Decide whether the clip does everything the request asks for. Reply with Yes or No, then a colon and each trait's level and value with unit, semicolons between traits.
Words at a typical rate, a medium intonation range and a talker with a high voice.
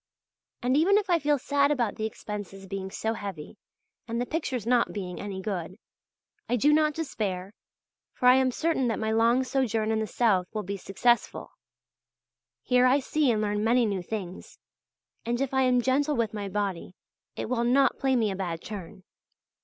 Yes: average, 185 wpm; average, 4.6 semitones; high, 230 Hz